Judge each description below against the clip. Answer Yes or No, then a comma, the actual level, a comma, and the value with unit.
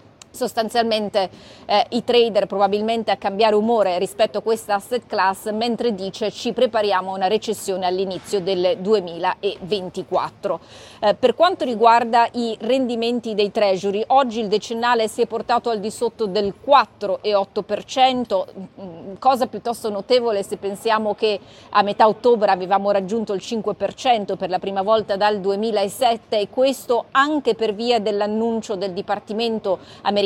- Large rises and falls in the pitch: No, average, 2.8 semitones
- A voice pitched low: No, high, 215 Hz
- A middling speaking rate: Yes, average, 140 wpm